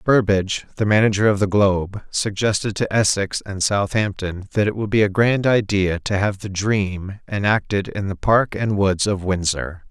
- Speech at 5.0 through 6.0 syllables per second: No, 4.7 syllables/s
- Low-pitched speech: Yes, low, 100 Hz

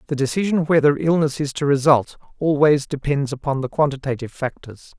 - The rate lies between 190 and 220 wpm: No, average, 155 wpm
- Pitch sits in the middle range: Yes, medium, 145 Hz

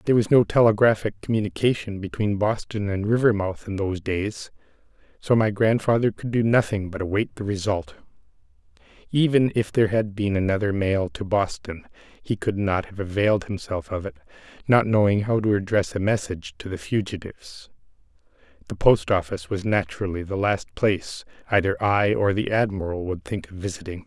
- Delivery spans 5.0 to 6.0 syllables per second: Yes, 5.5 syllables/s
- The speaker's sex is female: No, male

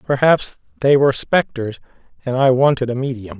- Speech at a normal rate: Yes, average, 160 wpm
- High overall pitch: No, low, 130 Hz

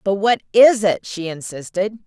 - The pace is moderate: Yes, average, 175 wpm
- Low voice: No, high, 200 Hz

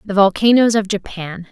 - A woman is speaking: Yes, female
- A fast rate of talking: No, average, 160 wpm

